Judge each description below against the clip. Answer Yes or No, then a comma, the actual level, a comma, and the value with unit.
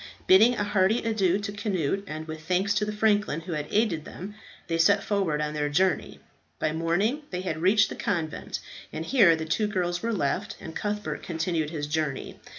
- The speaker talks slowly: No, average, 195 wpm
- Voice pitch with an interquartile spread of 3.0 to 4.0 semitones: No, average, 4.5 semitones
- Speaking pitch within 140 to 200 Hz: Yes, medium, 185 Hz